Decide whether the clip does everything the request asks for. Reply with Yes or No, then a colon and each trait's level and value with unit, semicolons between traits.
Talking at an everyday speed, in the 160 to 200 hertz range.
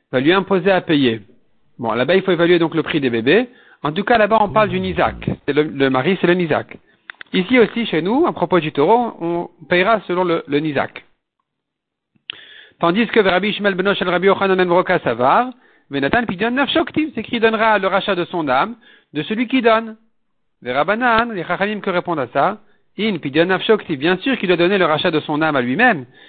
Yes: average, 210 wpm; high, 190 Hz